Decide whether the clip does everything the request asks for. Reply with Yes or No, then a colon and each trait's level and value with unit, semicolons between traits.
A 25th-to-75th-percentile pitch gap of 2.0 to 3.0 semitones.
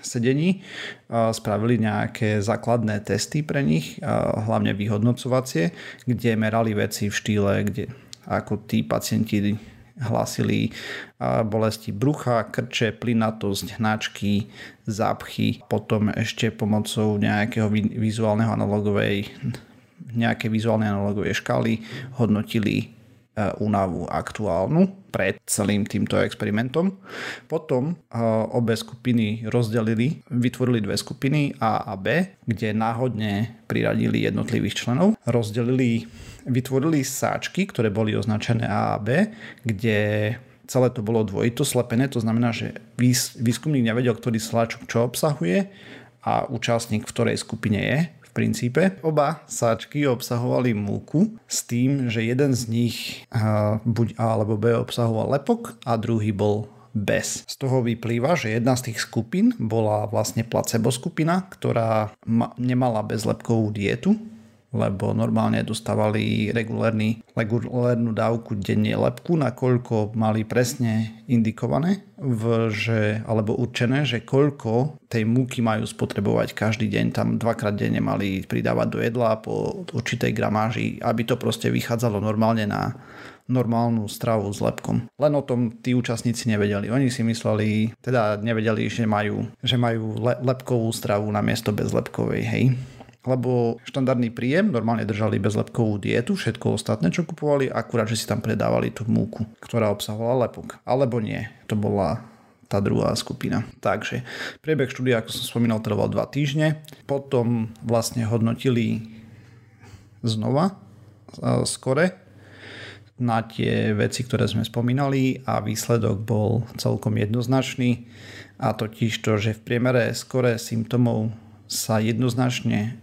Yes: narrow, 2.4 semitones